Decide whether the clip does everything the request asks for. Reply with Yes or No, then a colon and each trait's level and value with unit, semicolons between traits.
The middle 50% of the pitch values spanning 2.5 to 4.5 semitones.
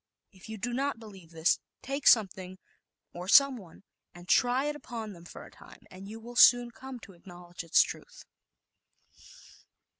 No: average, 5.2 semitones